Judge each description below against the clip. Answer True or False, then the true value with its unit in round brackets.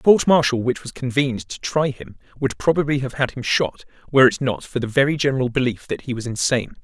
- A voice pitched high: False (130 Hz)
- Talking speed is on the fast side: True (235 wpm)